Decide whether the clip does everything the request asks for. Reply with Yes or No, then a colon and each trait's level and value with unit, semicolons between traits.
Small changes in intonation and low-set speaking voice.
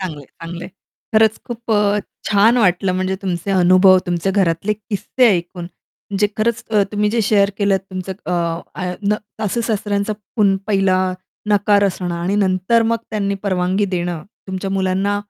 No: narrow, 2.1 semitones; high, 195 Hz